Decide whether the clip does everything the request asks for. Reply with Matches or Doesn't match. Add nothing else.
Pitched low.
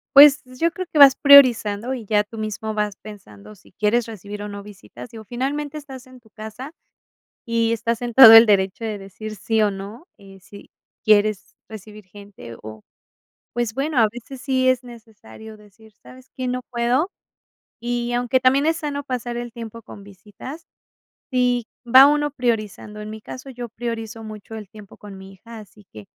Doesn't match